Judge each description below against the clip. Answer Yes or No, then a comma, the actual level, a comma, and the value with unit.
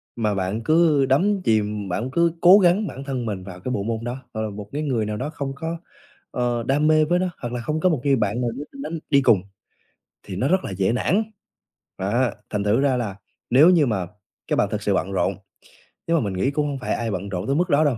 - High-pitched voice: No, low, 125 Hz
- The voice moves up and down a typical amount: No, wide, 6.4 semitones